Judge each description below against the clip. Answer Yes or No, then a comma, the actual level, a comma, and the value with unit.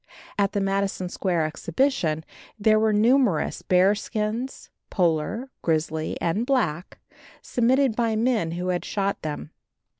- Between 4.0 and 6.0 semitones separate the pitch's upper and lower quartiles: Yes, average, 5.1 semitones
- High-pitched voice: Yes, high, 200 Hz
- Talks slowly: Yes, slow, 125 wpm